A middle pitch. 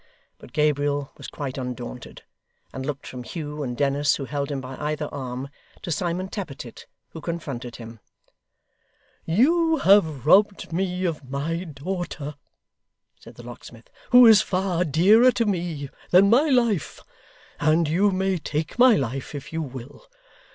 Yes: medium, 155 Hz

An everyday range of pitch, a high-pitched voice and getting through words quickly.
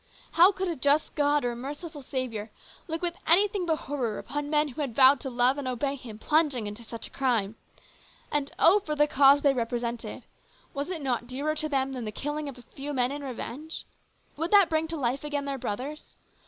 Yes: average, 3.6 semitones; very high, 280 Hz; fast, 215 wpm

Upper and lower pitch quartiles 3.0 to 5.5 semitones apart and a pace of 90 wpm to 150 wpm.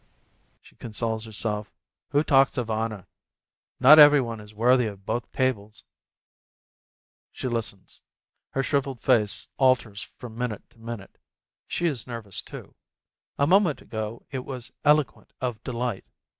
Yes: average, 3.5 semitones; average, 140 wpm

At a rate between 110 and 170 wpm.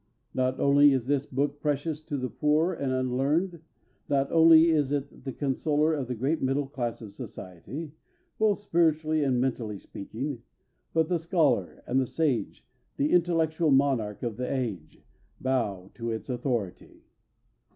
Yes: average, 150 wpm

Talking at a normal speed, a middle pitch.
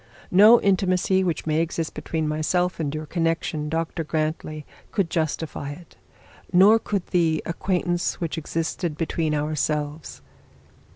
No: slow, 125 wpm; medium, 165 Hz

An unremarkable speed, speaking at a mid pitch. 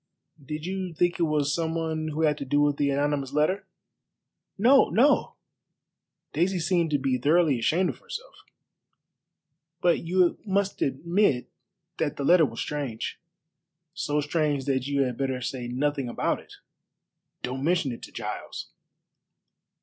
Yes: average, 150 wpm; medium, 150 Hz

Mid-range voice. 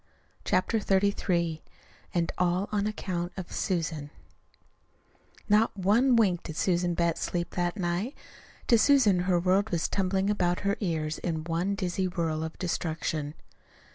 Yes: medium, 180 Hz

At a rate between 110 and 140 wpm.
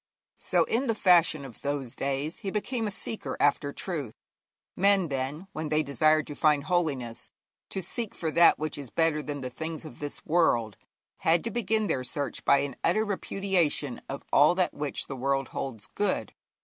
No: average, 185 wpm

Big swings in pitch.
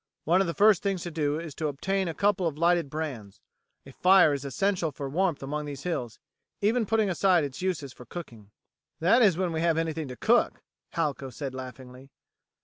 No: average, 4.9 semitones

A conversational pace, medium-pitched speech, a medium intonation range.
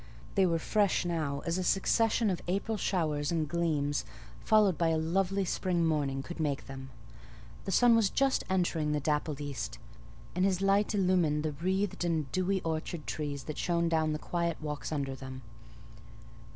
Yes: average, 170 wpm; medium, 170 Hz; average, 4.0 semitones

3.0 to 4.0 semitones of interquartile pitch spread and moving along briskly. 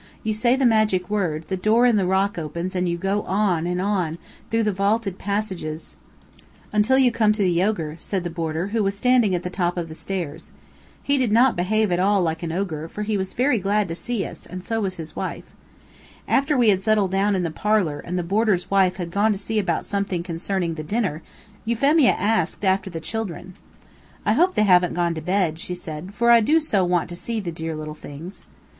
Yes: average, 3.7 semitones; fast, 225 wpm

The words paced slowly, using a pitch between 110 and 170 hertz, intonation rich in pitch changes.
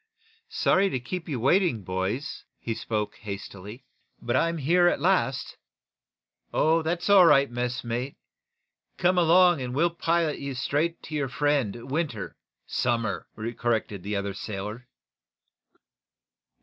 Yes: slow, 130 wpm; low, 135 Hz; wide, 6.8 semitones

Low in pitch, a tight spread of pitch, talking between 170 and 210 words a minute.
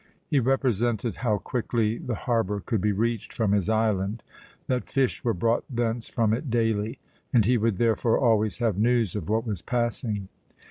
Yes: low, 115 Hz; narrow, 2.3 semitones; average, 175 wpm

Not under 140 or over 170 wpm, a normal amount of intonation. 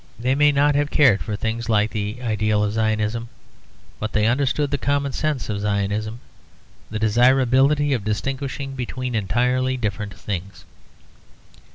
Yes: average, 145 wpm; average, 4.1 semitones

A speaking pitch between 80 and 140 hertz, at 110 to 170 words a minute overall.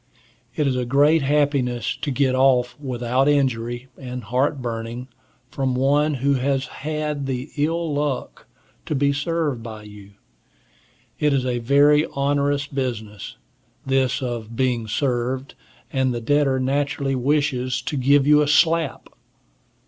Yes: low, 135 Hz; average, 140 wpm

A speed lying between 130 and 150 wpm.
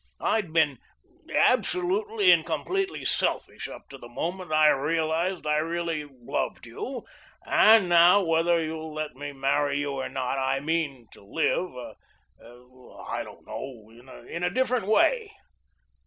Yes: average, 140 wpm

